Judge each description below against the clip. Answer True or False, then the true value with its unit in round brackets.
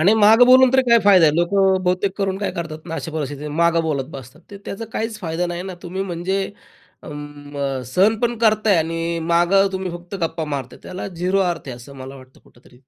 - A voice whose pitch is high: False (175 Hz)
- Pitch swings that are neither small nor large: True (4.5 semitones)